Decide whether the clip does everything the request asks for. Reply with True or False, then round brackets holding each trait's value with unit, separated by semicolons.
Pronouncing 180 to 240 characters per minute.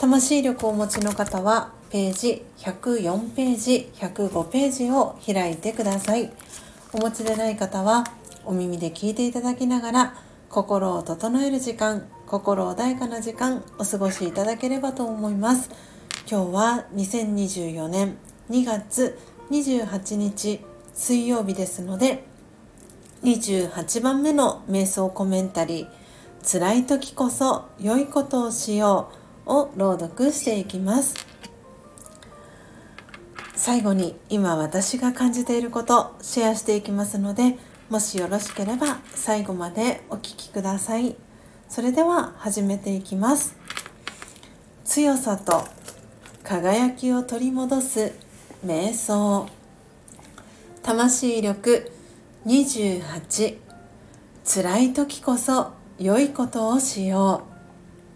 True (210 characters per minute)